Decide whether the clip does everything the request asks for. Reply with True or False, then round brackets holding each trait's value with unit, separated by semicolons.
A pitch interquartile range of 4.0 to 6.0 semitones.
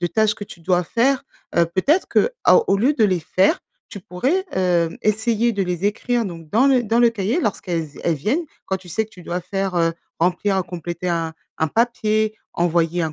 True (4.7 semitones)